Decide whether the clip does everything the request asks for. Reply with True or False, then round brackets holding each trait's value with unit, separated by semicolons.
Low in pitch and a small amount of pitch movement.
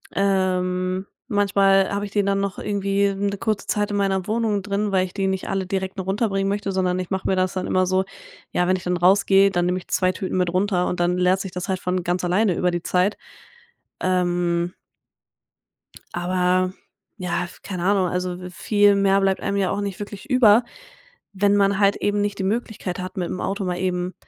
False (190 Hz; 1.6 semitones)